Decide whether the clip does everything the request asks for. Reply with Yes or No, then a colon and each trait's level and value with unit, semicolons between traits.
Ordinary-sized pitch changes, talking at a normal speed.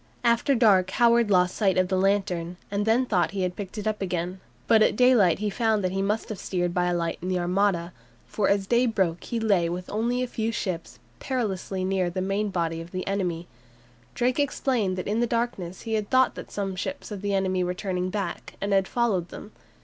No: average, 3.5 semitones; fast, 225 wpm